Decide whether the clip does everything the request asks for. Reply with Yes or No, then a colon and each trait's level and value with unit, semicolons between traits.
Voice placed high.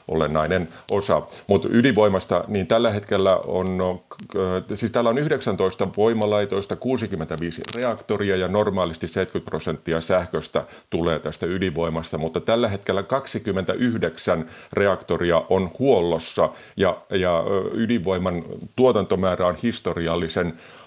No: very low, 95 Hz